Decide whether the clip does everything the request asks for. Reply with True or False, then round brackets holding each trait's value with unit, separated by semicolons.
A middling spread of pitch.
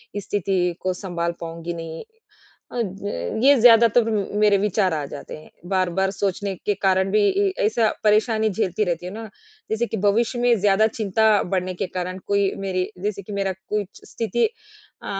True (3.0 semitones)